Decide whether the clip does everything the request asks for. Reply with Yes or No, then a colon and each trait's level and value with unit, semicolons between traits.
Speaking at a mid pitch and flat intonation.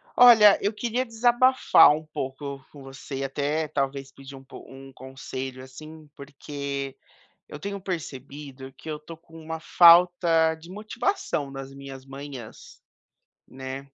No: medium, 145 Hz; average, 3.7 semitones